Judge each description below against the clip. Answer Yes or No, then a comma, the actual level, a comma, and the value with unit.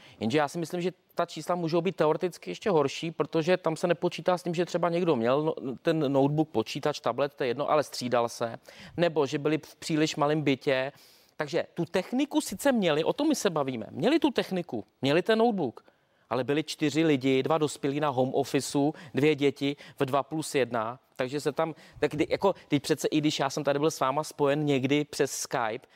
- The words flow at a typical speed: No, fast, 205 wpm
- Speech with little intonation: No, average, 3.6 semitones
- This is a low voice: No, medium, 155 Hz